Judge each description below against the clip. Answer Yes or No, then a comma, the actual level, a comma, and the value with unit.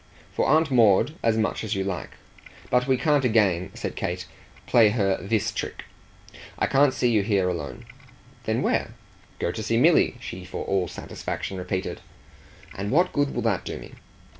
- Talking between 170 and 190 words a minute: Yes, average, 175 wpm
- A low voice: Yes, low, 110 Hz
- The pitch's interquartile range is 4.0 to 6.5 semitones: Yes, average, 4.7 semitones